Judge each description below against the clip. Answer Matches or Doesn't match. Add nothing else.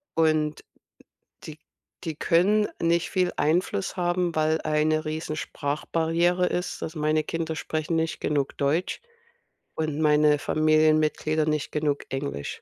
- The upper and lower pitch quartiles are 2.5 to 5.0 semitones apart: Doesn't match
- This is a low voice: Doesn't match